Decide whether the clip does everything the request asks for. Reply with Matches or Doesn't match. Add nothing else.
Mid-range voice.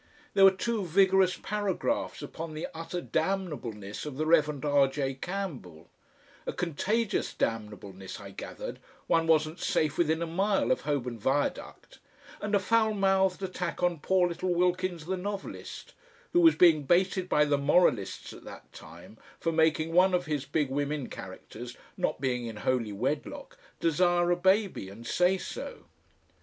Matches